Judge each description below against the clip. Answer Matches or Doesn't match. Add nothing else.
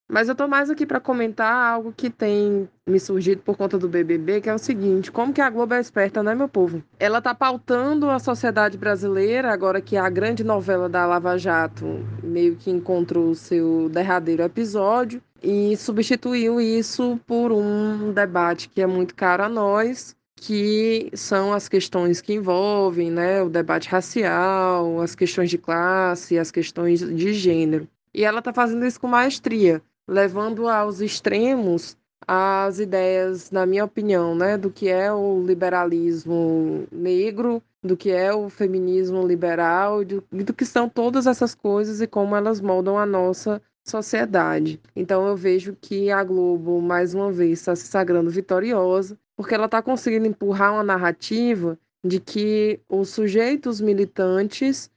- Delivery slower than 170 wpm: Matches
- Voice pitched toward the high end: Matches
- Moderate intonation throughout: Matches